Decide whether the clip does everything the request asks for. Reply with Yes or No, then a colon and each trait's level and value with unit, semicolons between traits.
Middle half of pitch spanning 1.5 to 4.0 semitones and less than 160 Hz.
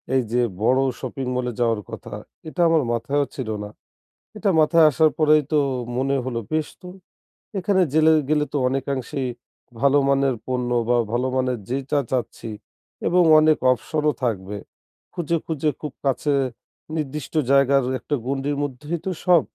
Yes: average, 3.3 semitones; medium, 140 Hz